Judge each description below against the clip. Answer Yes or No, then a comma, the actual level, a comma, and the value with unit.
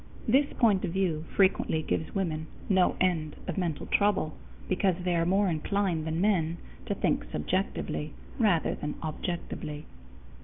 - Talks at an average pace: Yes, average, 145 wpm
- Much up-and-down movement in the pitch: No, average, 3.6 semitones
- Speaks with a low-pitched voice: No, medium, 175 Hz